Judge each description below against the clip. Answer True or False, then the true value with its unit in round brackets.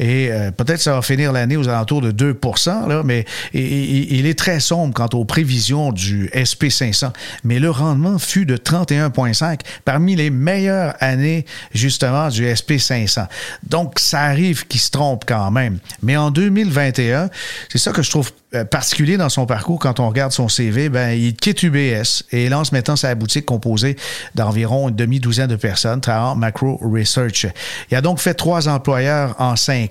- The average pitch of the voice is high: False (135 Hz)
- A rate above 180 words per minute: False (170 wpm)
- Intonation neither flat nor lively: True (4.0 semitones)